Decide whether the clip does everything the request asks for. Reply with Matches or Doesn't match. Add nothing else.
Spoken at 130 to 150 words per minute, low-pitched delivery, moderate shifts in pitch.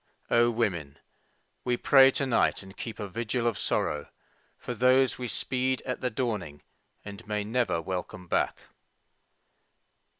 Matches